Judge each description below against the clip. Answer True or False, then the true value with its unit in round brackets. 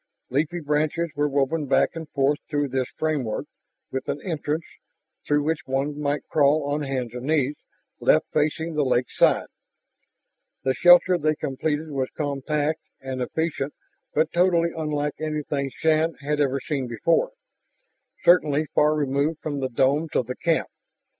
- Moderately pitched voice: True (150 Hz)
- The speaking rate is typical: True (145 wpm)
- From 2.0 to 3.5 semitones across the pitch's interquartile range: True (2.4 semitones)